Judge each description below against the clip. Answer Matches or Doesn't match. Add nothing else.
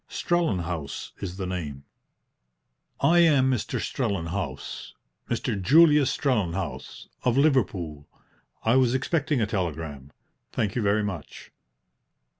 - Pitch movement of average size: Doesn't match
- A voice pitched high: Doesn't match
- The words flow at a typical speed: Doesn't match